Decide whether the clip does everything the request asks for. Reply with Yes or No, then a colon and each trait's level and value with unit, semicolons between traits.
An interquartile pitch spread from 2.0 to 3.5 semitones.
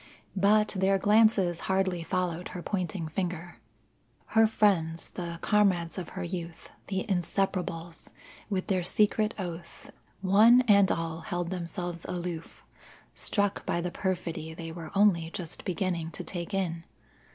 Yes: narrow, 2.6 semitones